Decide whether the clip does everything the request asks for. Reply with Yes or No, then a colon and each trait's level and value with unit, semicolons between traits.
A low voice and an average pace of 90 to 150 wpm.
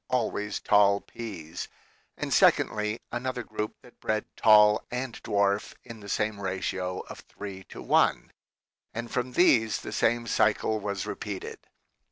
Yes: low, 105 Hz; average, 140 wpm